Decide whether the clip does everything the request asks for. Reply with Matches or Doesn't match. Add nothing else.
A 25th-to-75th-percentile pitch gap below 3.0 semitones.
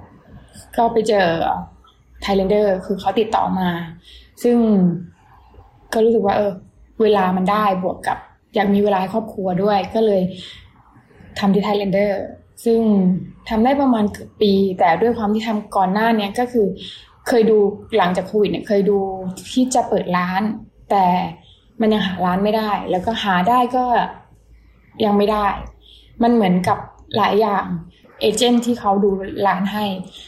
Matches